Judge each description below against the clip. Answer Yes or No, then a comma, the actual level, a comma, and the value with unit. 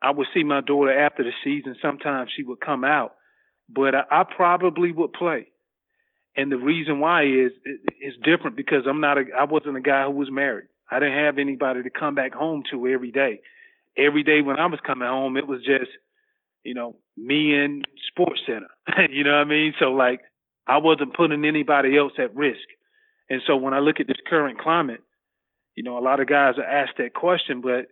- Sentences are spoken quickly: Yes, fast, 215 wpm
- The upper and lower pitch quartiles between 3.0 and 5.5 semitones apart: No, narrow, 2.5 semitones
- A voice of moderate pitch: Yes, medium, 145 Hz